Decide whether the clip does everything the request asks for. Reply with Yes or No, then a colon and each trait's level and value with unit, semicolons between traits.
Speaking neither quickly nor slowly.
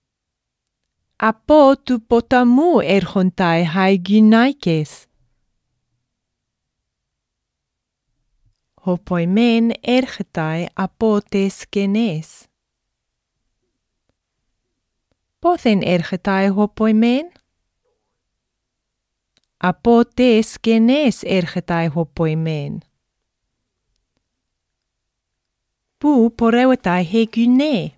No: slow, 50 wpm